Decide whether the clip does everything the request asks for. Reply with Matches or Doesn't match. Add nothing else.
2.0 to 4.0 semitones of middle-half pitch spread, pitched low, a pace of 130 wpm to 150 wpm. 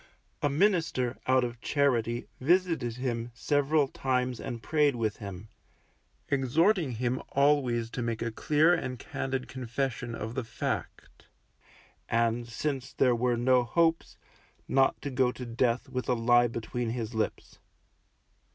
Matches